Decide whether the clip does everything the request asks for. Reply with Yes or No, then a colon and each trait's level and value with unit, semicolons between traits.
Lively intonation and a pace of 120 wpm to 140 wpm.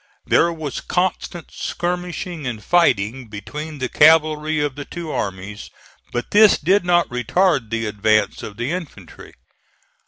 Yes: wide, 7.4 semitones; slow, 135 wpm